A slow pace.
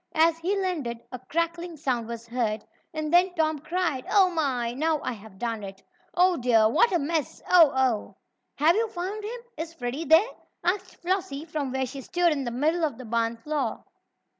No: average, 190 wpm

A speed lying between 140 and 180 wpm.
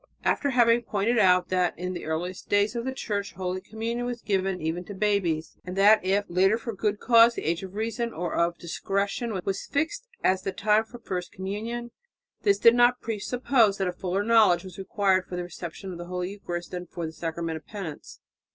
No: fast, 205 wpm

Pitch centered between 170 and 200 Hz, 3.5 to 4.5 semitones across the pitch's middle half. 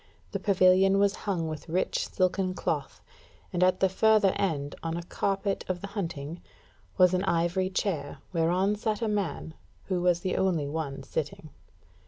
No: medium, 185 Hz; average, 2.9 semitones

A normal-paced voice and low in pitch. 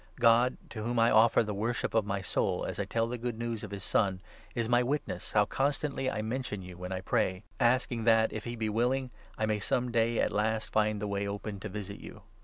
No: fast, 245 wpm; low, 110 Hz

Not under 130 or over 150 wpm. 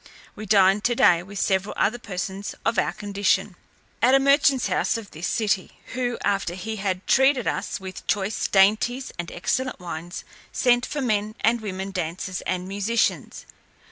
No: average, 160 wpm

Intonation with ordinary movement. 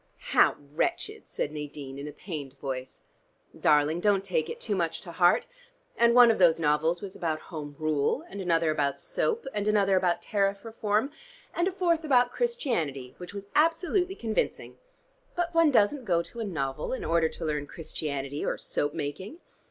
No: wide, 7.7 semitones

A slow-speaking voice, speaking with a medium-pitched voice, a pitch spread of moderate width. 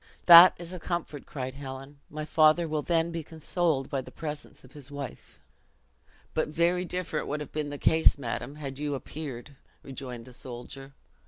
No: average, 175 wpm; medium, 150 Hz; average, 3.1 semitones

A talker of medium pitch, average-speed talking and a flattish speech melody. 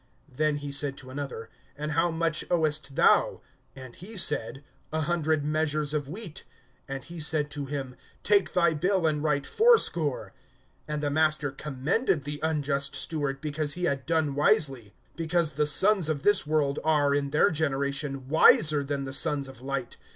Yes: medium, 150 Hz; average, 170 wpm; narrow, 2.3 semitones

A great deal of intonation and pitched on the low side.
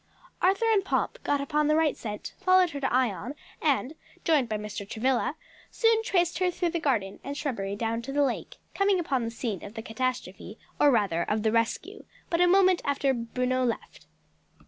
No: wide, 6.7 semitones; very high, 265 Hz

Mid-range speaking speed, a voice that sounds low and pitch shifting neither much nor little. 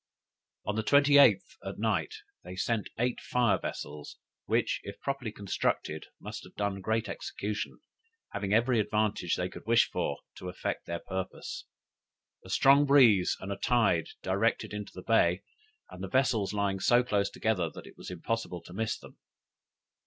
Yes: average, 160 wpm; low, 105 Hz; average, 3.9 semitones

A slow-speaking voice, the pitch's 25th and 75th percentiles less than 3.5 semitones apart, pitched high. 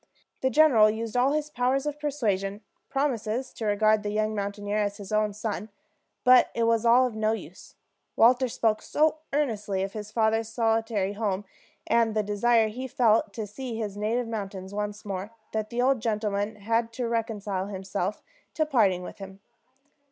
No: average, 175 wpm; narrow, 2.6 semitones; high, 220 Hz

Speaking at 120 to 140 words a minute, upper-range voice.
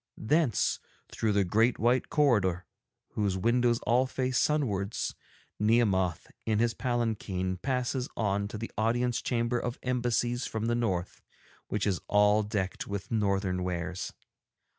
No: slow, 135 wpm; low, 110 Hz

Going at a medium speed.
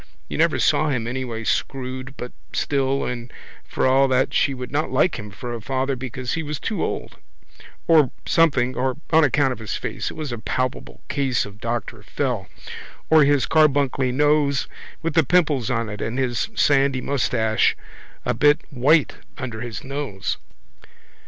Yes: average, 170 wpm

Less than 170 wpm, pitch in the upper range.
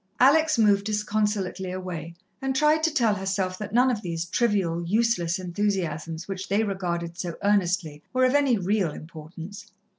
Yes: average, 155 wpm; high, 195 Hz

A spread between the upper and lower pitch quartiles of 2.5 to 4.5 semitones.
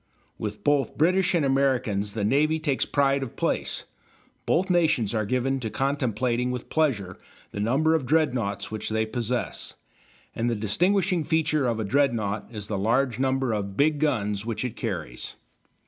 No: average, 5.1 semitones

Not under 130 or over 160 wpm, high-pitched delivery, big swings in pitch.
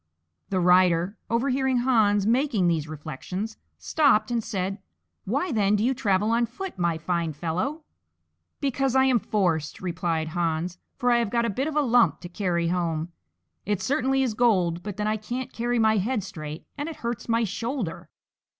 No: average, 175 wpm; high, 210 Hz; wide, 5.7 semitones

